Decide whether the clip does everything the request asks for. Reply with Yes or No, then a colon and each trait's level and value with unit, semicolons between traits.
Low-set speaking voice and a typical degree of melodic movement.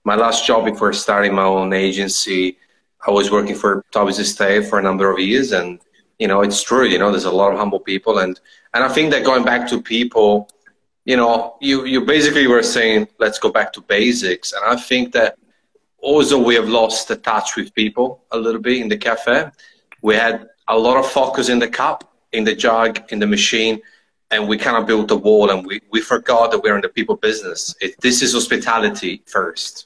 Yes: low, 115 Hz; average, 3.3 semitones